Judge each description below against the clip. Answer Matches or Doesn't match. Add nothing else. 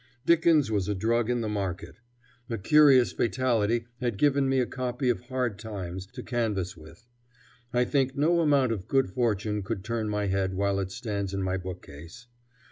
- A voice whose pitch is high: Doesn't match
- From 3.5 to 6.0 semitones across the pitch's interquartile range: Matches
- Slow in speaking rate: Doesn't match